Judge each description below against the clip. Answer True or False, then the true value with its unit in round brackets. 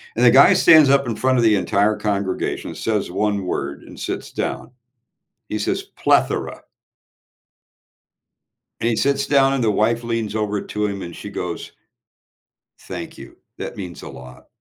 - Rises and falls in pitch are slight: False (3.2 semitones)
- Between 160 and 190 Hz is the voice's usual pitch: False (105 Hz)